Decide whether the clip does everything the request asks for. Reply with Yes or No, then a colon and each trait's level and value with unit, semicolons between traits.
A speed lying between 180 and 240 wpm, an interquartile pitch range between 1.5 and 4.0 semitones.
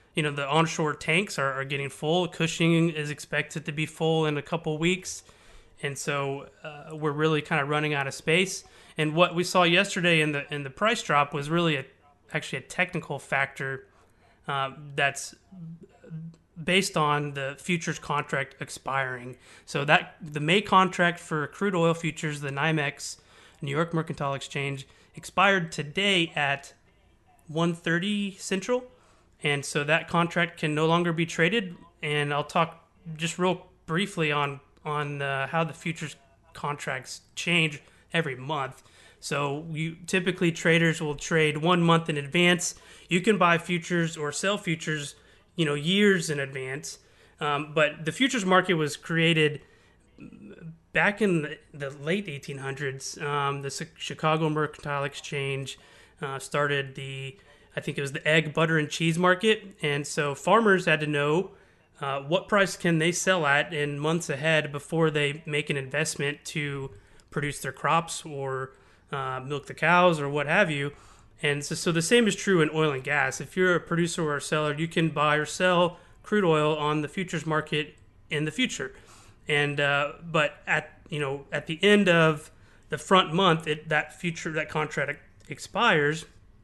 No: average, 165 wpm; average, 3.1 semitones